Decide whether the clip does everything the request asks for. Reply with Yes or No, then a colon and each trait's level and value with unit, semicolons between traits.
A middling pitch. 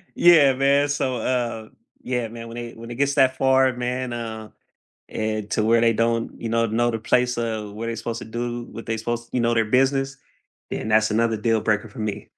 No: low, 115 Hz